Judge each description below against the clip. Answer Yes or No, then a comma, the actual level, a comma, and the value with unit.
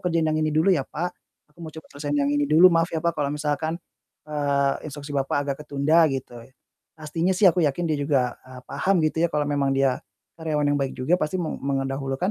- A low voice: No, medium, 150 Hz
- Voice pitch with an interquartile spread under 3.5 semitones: Yes, narrow, 2.6 semitones